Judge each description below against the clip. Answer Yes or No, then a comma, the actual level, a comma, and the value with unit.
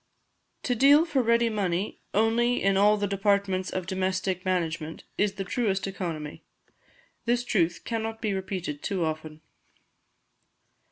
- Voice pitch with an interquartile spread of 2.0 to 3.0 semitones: No, average, 3.5 semitones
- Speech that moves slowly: Yes, slow, 130 wpm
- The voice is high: Yes, high, 195 Hz